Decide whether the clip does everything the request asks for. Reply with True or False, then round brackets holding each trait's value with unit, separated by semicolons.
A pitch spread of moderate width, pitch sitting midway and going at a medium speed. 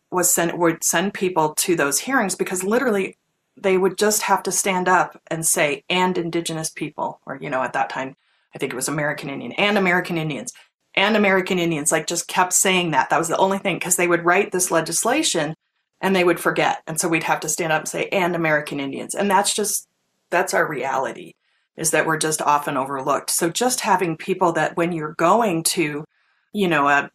False (3.2 semitones; 175 Hz; 210 wpm)